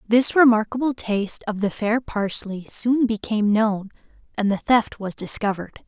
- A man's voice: No, female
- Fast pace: No, average, 155 wpm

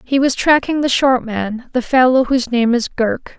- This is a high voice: Yes, very high, 250 Hz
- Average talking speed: No, fast, 215 wpm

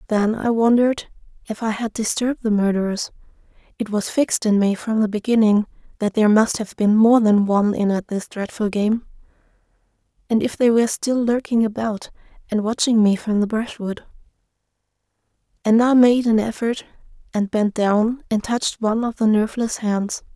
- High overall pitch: Yes, high, 220 Hz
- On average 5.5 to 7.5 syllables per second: No, 5.3 syllables/s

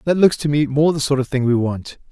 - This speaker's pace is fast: Yes, fast, 310 wpm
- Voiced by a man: Yes, male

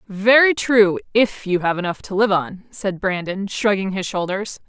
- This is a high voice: Yes, high, 205 Hz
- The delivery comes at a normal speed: Yes, average, 180 wpm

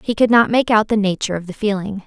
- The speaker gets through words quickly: Yes, fast, 290 wpm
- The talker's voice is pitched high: Yes, high, 210 Hz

